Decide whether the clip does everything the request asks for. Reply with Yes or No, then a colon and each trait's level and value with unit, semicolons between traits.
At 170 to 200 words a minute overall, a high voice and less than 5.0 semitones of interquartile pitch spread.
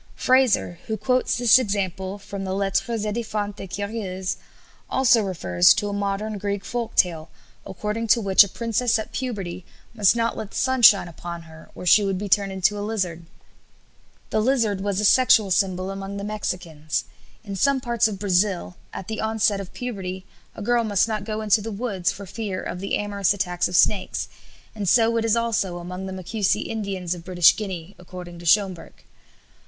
Yes: average, 185 wpm; high, 200 Hz; average, 2.9 semitones